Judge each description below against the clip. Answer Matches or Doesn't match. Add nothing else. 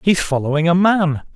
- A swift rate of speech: Doesn't match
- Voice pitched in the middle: Matches